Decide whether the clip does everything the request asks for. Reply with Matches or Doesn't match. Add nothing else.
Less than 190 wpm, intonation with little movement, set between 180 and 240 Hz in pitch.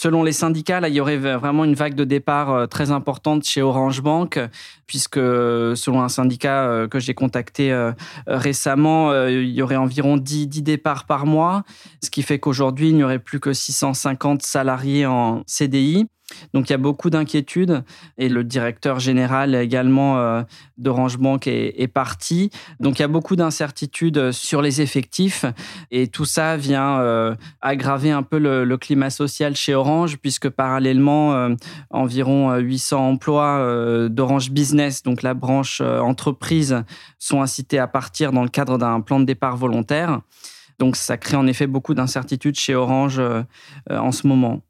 Doesn't match